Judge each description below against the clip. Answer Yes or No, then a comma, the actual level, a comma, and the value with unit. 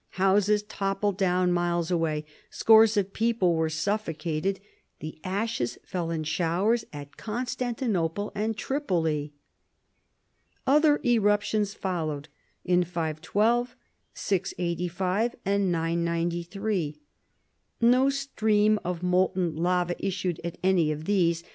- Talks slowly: Yes, slow, 105 wpm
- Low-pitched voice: No, medium, 185 Hz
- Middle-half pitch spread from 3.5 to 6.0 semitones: Yes, average, 3.9 semitones